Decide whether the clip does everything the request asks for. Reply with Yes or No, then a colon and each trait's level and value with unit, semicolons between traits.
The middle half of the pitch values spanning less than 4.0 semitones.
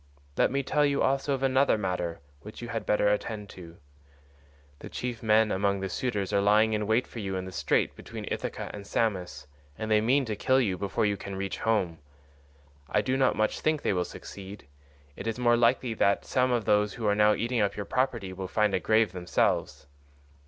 Yes: average, 3.3 semitones